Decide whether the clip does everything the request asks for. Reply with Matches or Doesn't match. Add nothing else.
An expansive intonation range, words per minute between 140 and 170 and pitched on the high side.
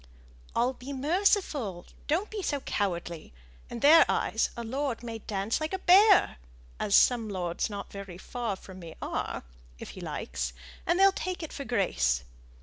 Matches